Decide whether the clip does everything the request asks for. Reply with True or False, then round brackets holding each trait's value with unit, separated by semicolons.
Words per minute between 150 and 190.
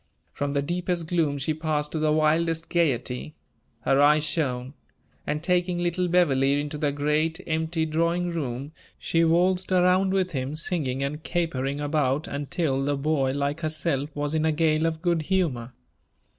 True (160 wpm)